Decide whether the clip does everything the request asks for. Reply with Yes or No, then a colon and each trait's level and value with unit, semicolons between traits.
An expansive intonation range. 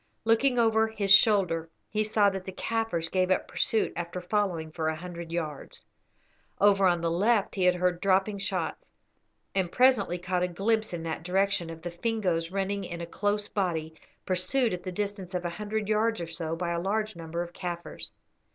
No: average, 3.3 semitones